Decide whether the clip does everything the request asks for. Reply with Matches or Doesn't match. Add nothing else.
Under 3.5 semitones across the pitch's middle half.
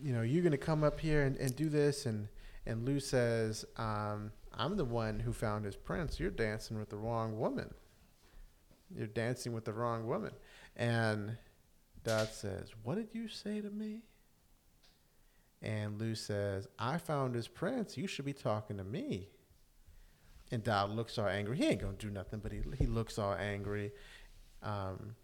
Doesn't match